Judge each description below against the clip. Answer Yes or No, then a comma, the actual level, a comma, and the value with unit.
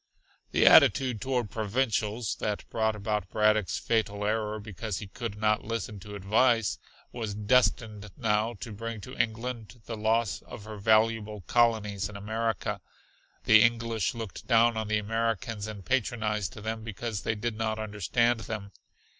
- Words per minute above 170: No, average, 150 wpm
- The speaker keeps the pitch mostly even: Yes, narrow, 1.6 semitones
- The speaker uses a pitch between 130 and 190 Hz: No, low, 110 Hz